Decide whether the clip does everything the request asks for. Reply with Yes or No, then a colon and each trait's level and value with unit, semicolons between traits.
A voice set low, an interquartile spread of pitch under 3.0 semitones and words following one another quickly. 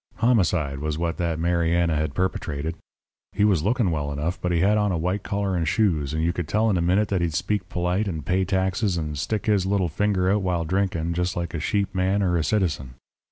No: very low, 90 Hz; average, 3.4 semitones; fast, 230 wpm